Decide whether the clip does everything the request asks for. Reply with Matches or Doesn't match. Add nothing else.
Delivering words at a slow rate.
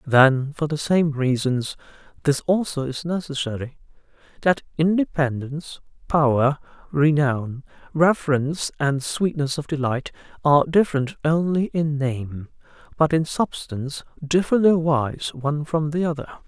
Matches